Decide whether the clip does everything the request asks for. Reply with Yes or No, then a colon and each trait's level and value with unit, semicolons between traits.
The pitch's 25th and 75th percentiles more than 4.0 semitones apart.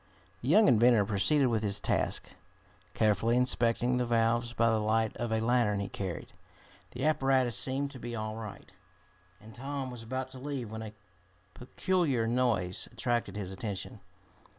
No: average, 2.9 semitones